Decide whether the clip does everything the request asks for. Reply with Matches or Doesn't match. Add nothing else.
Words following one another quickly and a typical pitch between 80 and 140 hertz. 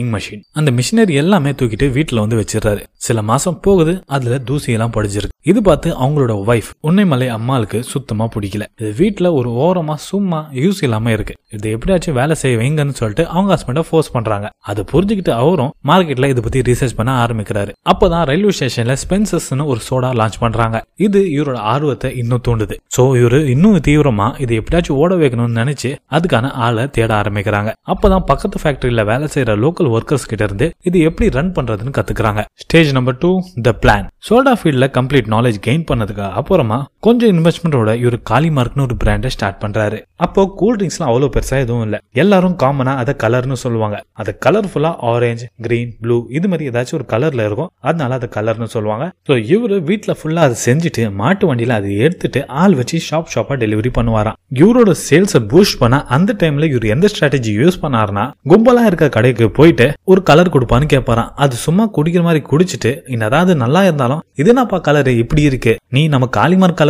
Matches